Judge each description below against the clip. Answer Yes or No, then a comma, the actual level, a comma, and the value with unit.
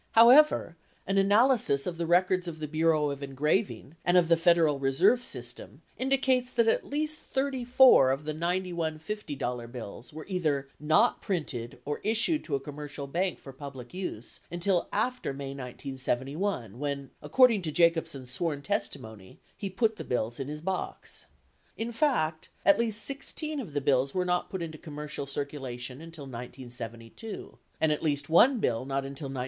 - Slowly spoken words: No, average, 165 wpm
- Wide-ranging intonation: Yes, wide, 6.3 semitones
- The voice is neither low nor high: Yes, medium, 155 Hz